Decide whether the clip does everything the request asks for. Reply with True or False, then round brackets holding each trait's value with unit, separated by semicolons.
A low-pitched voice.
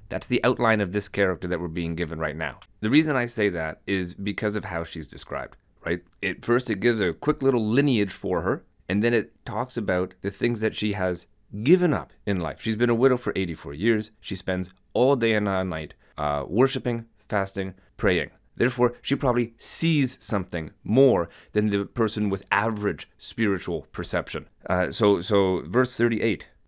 True (105 Hz)